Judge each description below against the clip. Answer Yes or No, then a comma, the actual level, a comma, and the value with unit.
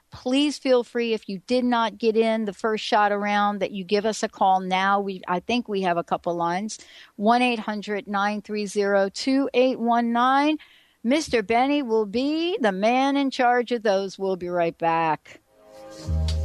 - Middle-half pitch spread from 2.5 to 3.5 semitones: No, average, 4.1 semitones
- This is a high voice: Yes, high, 210 Hz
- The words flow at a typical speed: Yes, average, 170 wpm